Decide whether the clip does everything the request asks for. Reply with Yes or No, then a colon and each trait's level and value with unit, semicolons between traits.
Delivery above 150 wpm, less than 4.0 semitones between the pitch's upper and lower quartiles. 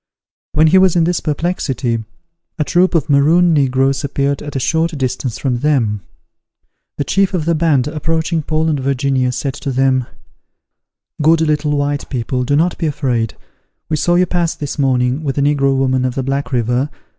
Yes: average, 180 wpm; average, 3.4 semitones